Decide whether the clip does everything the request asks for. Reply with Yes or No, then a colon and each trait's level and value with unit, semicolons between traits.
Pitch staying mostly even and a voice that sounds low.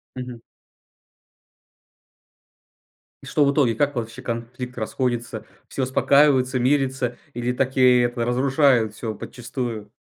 Yes: narrow, 2.0 semitones; low, 125 Hz